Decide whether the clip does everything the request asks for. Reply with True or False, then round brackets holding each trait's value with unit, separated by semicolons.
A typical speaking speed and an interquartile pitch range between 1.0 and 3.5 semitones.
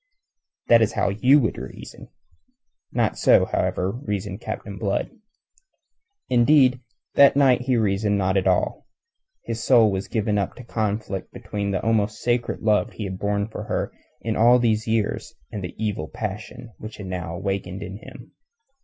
True (160 wpm; 2.9 semitones)